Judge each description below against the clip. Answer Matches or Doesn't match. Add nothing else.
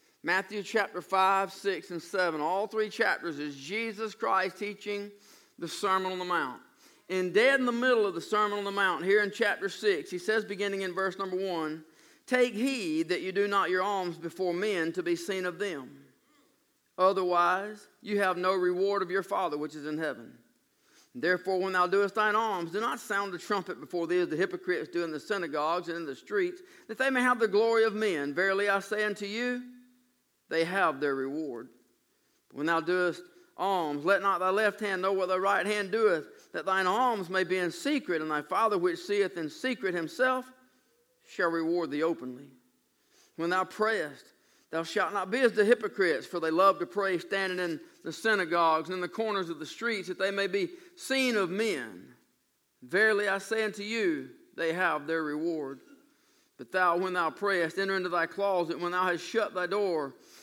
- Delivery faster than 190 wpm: Matches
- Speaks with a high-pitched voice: Matches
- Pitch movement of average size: Matches